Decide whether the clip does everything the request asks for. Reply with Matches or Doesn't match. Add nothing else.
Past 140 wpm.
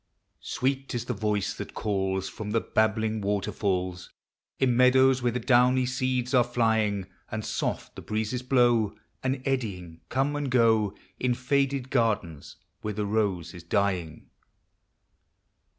Doesn't match